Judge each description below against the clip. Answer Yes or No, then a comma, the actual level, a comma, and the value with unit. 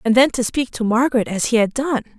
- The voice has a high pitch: Yes, high, 240 Hz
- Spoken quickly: Yes, fast, 275 wpm